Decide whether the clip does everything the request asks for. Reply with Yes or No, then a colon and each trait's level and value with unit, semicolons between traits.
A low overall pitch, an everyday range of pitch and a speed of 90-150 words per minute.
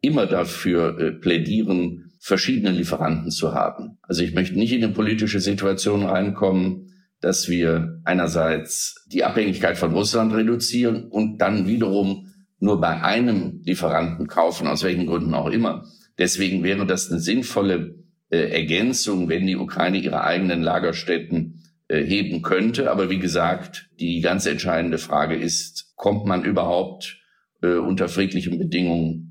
Yes: very low, 95 Hz; average, 3.5 semitones; average, 140 wpm